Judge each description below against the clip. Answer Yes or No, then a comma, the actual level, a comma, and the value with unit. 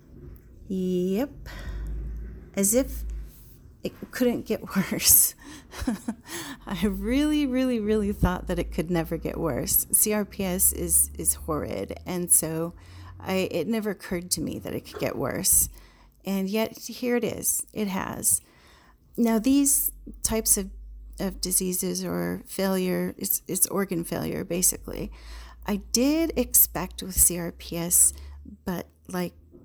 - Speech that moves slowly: Yes, slow, 125 wpm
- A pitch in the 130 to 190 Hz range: Yes, medium, 185 Hz